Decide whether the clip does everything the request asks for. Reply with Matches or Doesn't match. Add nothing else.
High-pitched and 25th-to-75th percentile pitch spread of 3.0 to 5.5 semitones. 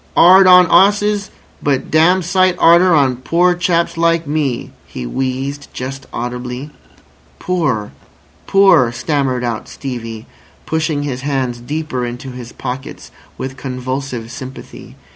Doesn't match